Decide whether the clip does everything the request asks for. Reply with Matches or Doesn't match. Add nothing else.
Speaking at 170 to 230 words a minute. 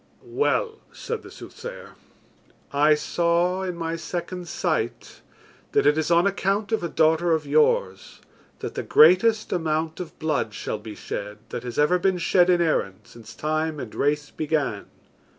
Doesn't match